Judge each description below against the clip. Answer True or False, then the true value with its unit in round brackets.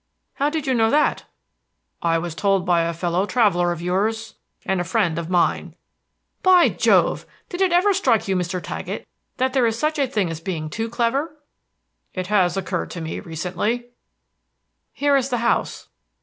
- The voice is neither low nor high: False (205 Hz)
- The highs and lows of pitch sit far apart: True (6.9 semitones)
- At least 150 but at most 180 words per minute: True (175 wpm)